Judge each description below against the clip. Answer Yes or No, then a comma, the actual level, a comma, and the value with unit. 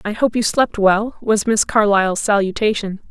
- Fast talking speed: No, average, 175 wpm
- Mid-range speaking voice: No, high, 210 Hz